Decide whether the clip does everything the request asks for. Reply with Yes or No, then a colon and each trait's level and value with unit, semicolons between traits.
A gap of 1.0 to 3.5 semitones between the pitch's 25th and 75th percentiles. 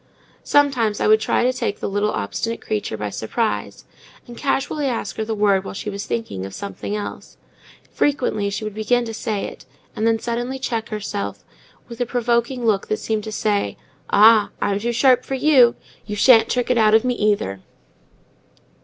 Yes: average, 2.8 semitones